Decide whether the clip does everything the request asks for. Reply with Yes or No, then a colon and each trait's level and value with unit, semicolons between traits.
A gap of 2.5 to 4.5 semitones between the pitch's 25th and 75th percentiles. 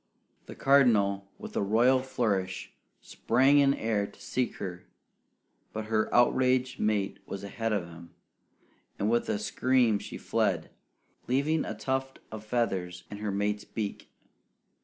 Yes: average, 4.2 semitones